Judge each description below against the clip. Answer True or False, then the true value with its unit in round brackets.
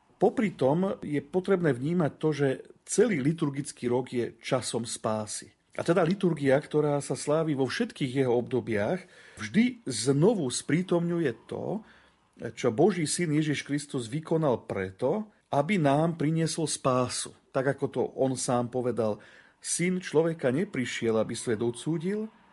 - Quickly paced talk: False (135 wpm)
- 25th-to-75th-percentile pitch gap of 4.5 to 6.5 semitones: True (4.9 semitones)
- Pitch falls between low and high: True (145 Hz)